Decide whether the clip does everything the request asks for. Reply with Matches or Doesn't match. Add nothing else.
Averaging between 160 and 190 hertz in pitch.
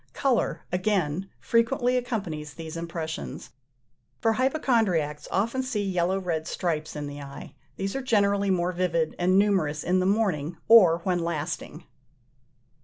Matches